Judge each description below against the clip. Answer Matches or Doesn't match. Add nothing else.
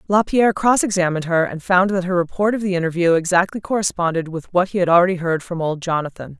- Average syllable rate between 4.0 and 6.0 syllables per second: Doesn't match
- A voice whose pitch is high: Doesn't match